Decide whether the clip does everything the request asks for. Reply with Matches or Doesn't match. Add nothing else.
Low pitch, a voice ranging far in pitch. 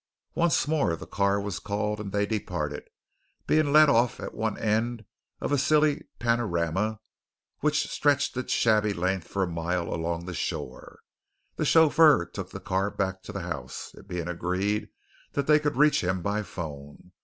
Matches